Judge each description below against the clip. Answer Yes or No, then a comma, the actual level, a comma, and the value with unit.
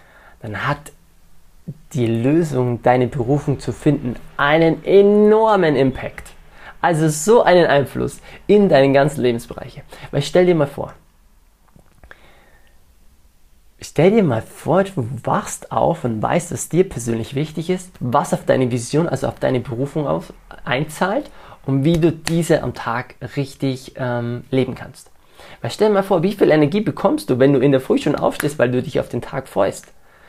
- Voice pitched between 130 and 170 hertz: Yes, low, 135 Hz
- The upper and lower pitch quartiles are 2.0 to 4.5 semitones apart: No, average, 5.2 semitones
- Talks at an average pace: Yes, average, 160 wpm